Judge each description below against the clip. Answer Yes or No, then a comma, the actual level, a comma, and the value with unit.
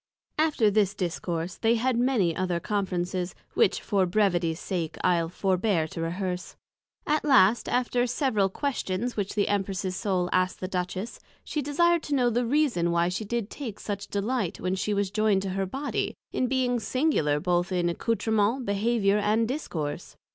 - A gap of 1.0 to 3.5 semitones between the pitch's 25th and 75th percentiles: No, average, 4.7 semitones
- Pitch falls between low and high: No, high, 200 Hz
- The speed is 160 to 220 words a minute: Yes, average, 165 wpm